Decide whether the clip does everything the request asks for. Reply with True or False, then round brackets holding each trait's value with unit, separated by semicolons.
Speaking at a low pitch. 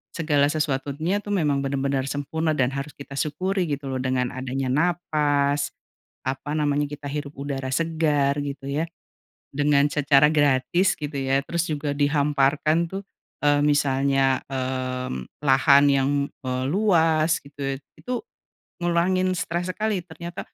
False (145 Hz)